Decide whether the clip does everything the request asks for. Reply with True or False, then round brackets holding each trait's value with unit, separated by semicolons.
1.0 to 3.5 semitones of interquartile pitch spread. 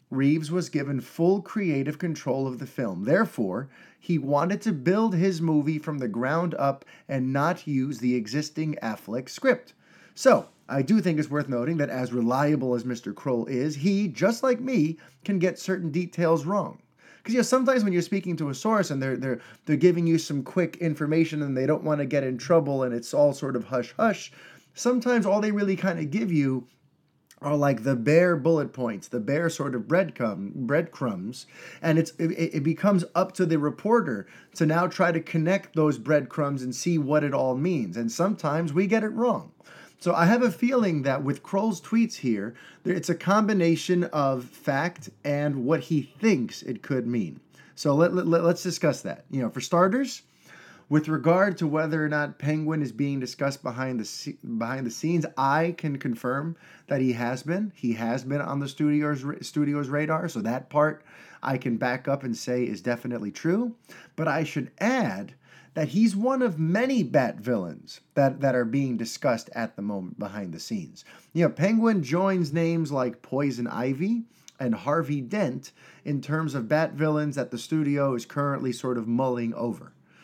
False (4.9 semitones)